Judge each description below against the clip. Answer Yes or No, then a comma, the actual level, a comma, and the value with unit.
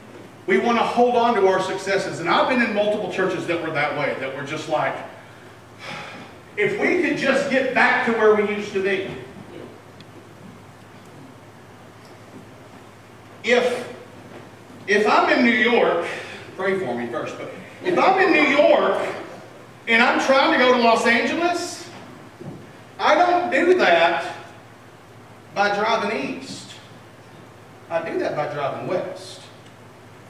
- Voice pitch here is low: No, high, 195 Hz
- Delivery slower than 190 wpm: Yes, average, 140 wpm